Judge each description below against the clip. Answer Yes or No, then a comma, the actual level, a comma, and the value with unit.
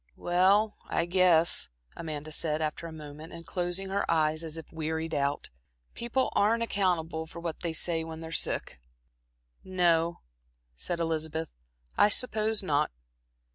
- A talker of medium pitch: Yes, medium, 165 Hz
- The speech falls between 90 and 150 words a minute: Yes, average, 140 wpm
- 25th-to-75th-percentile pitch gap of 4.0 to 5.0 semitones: No, narrow, 2.5 semitones